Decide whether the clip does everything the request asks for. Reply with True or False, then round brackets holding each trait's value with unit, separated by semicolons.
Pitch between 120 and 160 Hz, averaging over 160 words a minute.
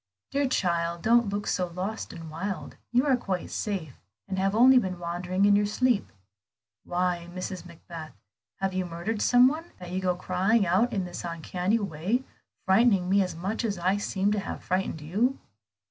False (190 Hz; 180 wpm)